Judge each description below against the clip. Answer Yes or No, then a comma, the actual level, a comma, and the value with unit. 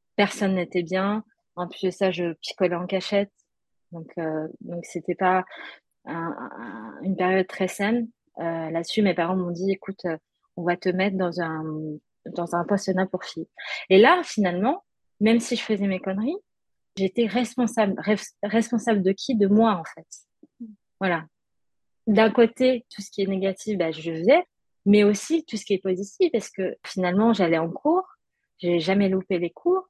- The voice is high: Yes, high, 195 Hz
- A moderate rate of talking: Yes, average, 180 wpm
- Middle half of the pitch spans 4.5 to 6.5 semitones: No, average, 3.7 semitones